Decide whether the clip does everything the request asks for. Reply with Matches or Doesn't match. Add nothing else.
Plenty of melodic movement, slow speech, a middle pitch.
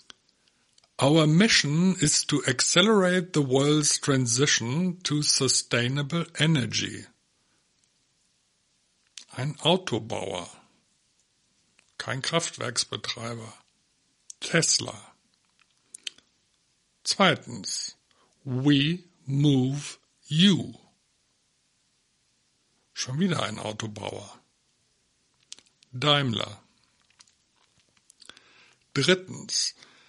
Doesn't match